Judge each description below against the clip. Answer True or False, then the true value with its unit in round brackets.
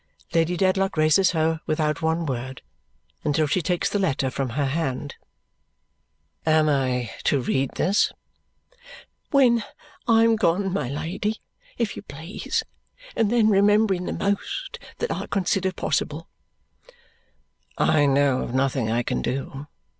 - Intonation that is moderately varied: False (6.1 semitones)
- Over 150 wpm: False (135 wpm)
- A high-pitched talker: False (160 Hz)